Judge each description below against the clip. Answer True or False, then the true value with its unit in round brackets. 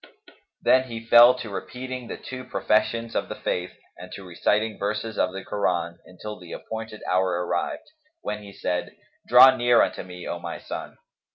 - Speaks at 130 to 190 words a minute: True (175 wpm)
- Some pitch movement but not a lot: True (4.5 semitones)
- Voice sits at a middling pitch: False (105 Hz)